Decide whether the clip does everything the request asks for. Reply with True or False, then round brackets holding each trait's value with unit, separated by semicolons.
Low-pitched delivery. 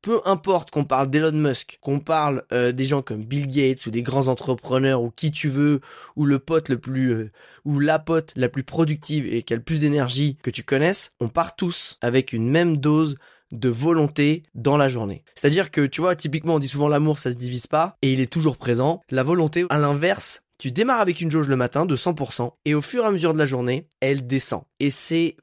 False (145 Hz)